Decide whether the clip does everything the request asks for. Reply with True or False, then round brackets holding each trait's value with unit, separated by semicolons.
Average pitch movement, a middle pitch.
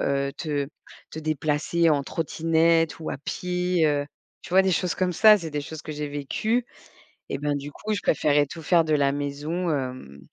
True (3.0 semitones; 155 Hz)